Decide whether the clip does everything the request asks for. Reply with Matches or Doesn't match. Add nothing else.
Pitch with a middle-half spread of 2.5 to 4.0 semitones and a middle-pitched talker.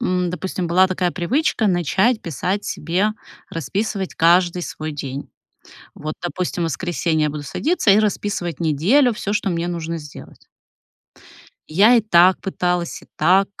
Matches